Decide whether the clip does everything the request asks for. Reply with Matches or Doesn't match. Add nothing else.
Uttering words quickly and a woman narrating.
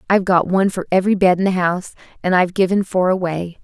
Matches